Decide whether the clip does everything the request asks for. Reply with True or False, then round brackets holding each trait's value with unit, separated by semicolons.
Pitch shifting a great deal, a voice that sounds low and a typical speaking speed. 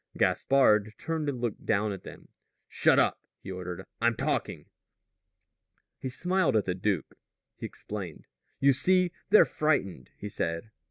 True (6.7 semitones; 110 Hz; 145 wpm)